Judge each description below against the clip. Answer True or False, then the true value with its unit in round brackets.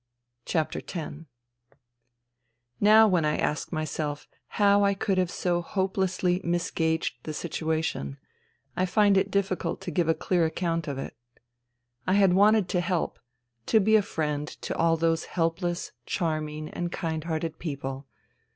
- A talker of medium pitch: True (170 Hz)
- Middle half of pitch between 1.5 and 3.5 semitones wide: True (3.2 semitones)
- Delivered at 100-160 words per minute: True (140 wpm)